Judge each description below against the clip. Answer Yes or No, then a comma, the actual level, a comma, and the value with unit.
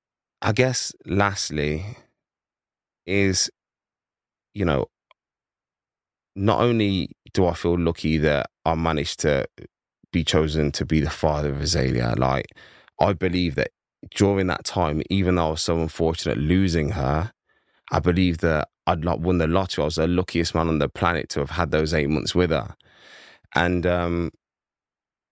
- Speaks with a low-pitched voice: Yes, very low, 85 Hz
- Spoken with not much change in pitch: No, average, 3.1 semitones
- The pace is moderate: Yes, average, 150 wpm